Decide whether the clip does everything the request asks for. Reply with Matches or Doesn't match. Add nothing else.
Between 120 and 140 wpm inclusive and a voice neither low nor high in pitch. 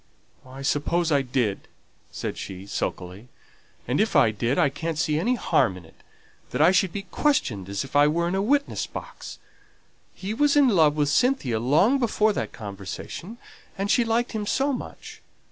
Doesn't match